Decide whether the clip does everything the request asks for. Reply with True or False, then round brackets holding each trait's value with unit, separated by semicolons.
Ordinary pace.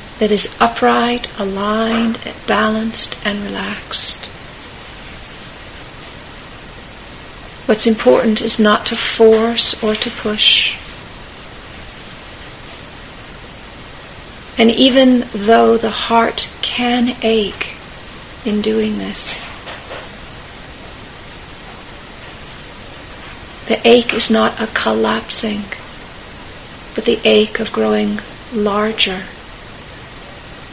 False (75 wpm)